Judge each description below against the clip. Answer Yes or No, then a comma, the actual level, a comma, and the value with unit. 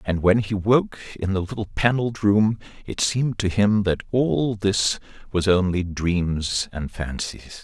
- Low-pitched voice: Yes, low, 100 Hz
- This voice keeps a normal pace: Yes, average, 165 wpm